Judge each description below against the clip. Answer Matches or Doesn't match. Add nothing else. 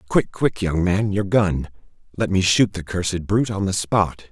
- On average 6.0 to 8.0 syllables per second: Doesn't match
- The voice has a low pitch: Matches